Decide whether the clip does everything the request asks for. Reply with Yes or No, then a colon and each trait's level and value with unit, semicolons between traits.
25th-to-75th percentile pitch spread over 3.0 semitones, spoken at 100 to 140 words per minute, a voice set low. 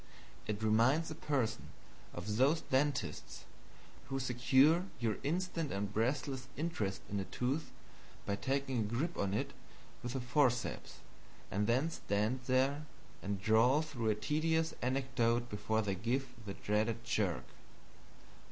Yes: average, 4.6 semitones; slow, 135 wpm; low, 125 Hz